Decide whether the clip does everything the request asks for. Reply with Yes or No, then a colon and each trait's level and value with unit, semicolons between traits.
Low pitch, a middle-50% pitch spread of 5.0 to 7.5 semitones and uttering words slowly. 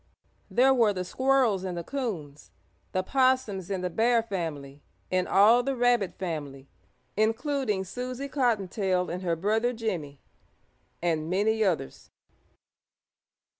No: high, 200 Hz; wide, 5.5 semitones; slow, 125 wpm